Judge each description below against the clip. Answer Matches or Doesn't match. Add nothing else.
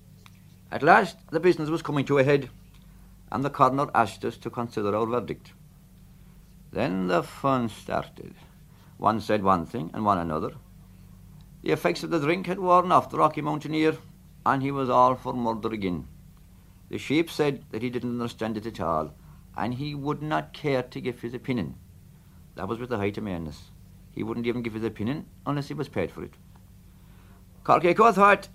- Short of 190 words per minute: Matches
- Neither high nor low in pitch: Doesn't match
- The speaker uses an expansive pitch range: Matches